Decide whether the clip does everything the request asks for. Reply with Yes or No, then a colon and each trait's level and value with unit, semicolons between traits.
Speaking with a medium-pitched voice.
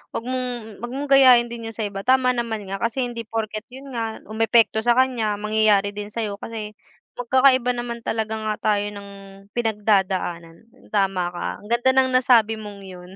No: high, 225 Hz